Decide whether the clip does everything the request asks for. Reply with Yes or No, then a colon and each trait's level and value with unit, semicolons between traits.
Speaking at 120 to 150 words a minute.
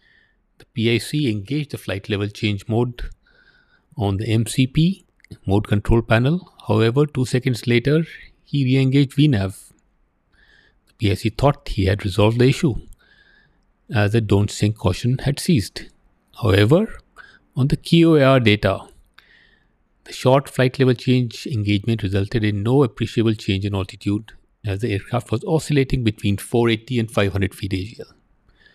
Yes: slow, 135 wpm